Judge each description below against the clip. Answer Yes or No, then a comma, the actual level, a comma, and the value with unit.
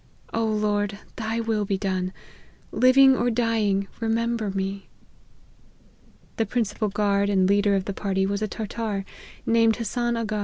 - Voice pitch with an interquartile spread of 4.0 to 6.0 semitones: No, narrow, 2.4 semitones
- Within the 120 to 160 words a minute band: Yes, average, 150 wpm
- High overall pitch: Yes, high, 210 Hz